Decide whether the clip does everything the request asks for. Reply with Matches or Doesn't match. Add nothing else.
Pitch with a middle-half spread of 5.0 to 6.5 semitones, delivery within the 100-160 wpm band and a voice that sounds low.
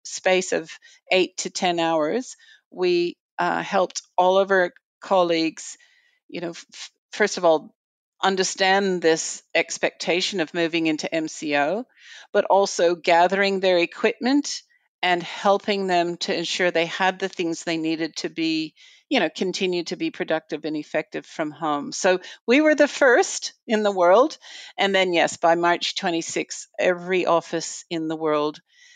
Doesn't match